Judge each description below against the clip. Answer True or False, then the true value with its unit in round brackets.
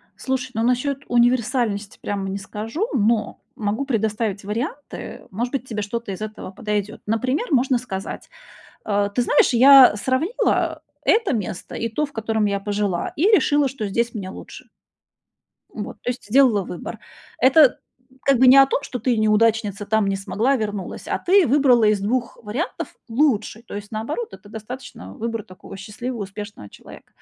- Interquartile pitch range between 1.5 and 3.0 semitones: False (3.9 semitones)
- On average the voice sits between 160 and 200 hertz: False (225 Hz)